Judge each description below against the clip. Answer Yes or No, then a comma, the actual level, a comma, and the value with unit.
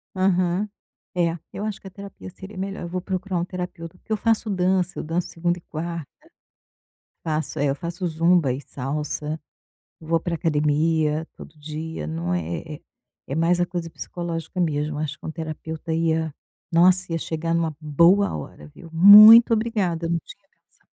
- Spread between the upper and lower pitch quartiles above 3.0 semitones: No, average, 2.7 semitones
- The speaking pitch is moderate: Yes, medium, 165 Hz